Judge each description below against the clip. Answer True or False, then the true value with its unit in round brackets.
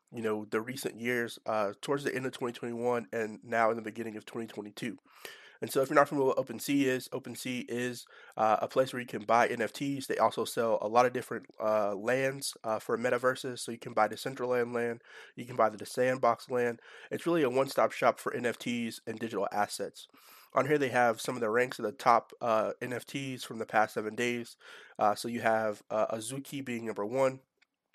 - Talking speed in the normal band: False (215 wpm)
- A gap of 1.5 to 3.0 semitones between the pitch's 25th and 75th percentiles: True (2.5 semitones)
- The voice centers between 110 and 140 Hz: True (120 Hz)